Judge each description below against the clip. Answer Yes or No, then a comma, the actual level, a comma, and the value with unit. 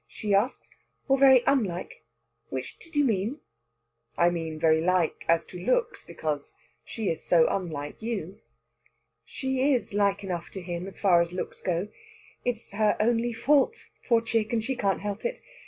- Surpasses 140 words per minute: Yes, average, 170 wpm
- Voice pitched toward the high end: Yes, high, 200 Hz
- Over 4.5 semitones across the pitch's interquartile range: Yes, wide, 5.6 semitones